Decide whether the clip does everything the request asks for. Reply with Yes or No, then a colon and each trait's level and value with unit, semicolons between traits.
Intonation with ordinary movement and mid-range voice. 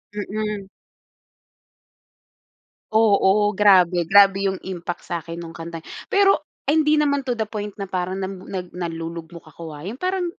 No: average, 4.0 semitones; high, 195 Hz